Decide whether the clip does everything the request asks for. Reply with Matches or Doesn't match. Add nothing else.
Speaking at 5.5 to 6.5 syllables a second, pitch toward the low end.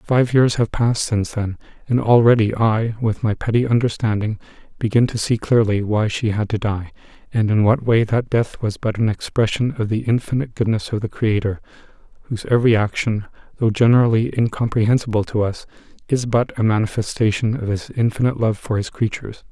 Matches